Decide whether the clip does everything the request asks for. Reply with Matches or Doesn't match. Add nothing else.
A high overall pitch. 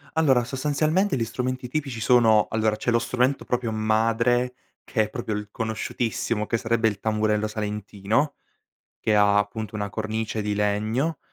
Doesn't match